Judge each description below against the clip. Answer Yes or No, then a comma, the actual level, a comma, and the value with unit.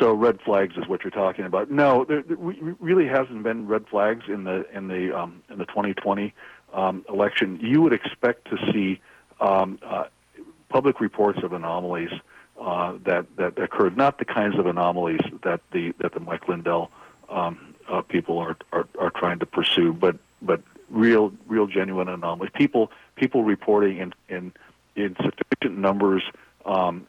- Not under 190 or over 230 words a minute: No, average, 170 wpm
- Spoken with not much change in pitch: No, average, 3.1 semitones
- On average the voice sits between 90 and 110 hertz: Yes, low, 100 Hz